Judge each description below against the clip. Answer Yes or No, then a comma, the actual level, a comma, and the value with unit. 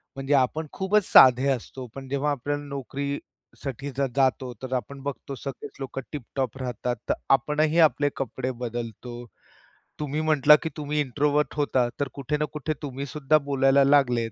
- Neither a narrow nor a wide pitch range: No, narrow, 2.2 semitones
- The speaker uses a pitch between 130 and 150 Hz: Yes, medium, 140 Hz